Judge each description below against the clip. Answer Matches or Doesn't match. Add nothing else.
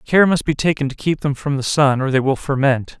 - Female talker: Doesn't match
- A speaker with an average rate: Doesn't match